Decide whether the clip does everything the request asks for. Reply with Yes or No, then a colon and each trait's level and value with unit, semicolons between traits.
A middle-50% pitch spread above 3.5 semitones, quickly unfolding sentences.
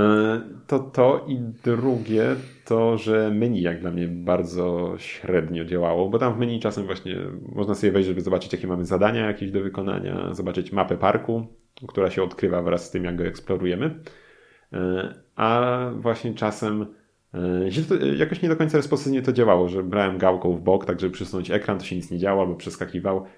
Yes: average, 4.1 semitones; fast, 175 wpm